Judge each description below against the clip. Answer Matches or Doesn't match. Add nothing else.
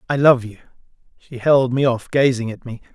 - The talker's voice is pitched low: Matches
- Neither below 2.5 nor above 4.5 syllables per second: Doesn't match